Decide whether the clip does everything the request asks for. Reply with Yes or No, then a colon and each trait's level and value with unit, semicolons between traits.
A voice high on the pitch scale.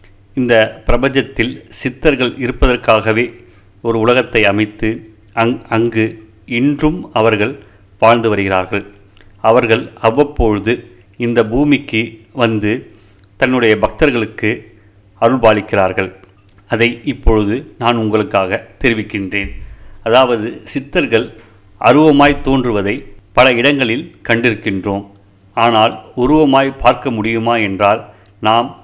No: low, 110 Hz